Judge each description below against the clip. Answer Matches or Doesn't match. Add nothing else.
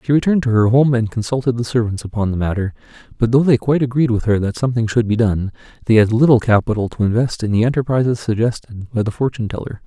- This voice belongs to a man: Matches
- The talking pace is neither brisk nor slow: Doesn't match